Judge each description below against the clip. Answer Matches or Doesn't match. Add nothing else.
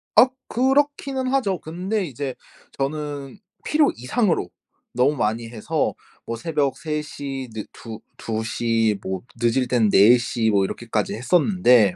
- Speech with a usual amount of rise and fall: Doesn't match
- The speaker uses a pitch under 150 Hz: Matches